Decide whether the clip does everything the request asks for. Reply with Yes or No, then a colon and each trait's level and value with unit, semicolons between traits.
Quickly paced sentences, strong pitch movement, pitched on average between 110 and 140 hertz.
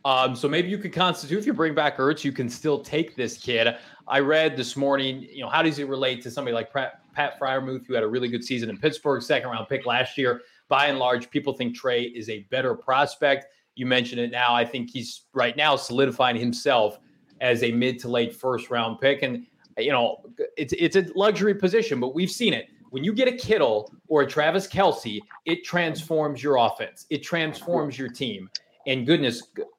No: fast, 210 wpm; average, 4.8 semitones; low, 135 Hz